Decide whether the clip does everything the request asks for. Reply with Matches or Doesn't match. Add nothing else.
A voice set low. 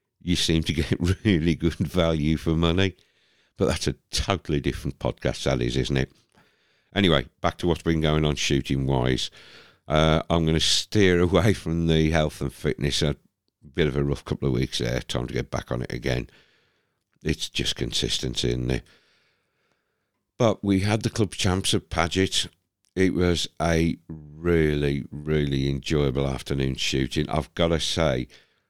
Matches